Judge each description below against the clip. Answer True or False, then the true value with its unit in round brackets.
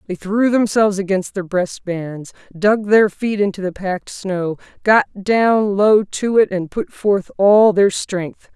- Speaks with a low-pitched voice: False (195 Hz)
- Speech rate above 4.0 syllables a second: False (3.9 syllables/s)